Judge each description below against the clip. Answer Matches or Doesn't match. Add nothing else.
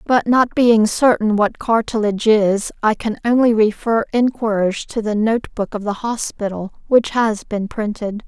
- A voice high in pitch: Matches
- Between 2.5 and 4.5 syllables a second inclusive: Matches